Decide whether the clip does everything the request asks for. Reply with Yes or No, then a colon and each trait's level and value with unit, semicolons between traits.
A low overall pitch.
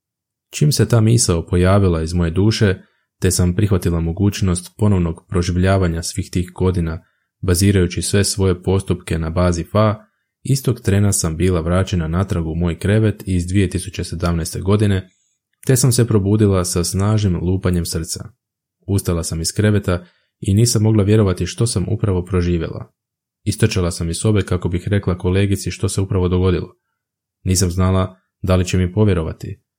Yes: very low, 95 Hz